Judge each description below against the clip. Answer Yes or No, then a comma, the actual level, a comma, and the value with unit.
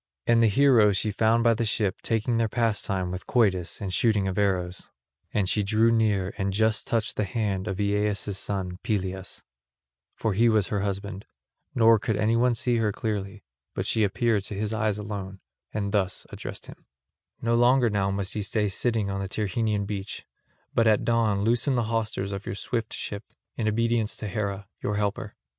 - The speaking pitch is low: Yes, low, 105 Hz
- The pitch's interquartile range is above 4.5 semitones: No, narrow, 2.4 semitones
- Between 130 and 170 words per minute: No, average, 185 wpm